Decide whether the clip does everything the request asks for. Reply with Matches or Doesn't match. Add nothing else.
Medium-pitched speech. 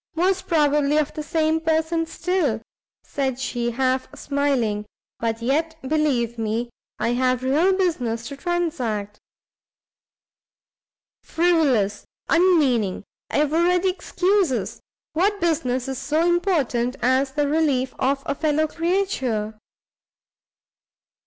Doesn't match